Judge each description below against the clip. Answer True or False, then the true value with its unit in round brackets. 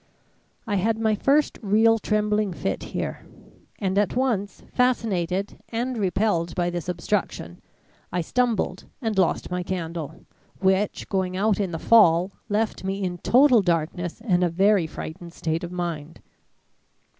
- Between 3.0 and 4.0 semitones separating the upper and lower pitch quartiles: True (3.7 semitones)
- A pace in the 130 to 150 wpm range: True (145 wpm)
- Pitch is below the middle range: False (190 Hz)